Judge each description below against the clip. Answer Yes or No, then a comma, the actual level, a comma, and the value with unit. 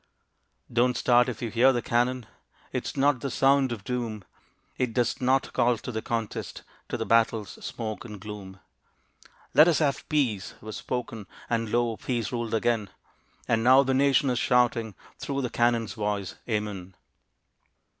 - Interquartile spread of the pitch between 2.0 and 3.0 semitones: Yes, average, 2.7 semitones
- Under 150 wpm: No, average, 165 wpm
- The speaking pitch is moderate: No, low, 120 Hz